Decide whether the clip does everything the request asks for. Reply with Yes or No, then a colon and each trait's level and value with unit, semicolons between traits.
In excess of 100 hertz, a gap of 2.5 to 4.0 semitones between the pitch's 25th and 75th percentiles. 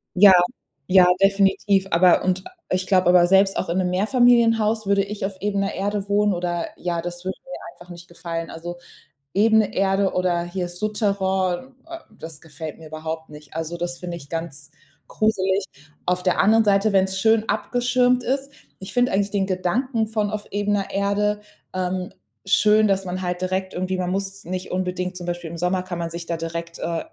Yes: high, 190 Hz; average, 2.8 semitones